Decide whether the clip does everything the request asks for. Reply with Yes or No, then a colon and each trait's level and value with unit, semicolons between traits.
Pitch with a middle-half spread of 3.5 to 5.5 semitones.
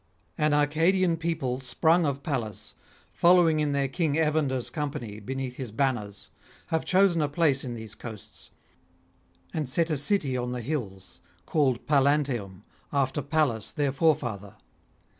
Yes: average, 4.3 semitones